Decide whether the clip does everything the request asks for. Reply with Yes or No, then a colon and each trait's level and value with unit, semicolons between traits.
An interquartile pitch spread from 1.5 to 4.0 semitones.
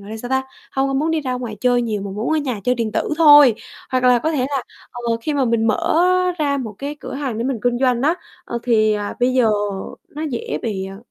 Yes: average, 3.4 semitones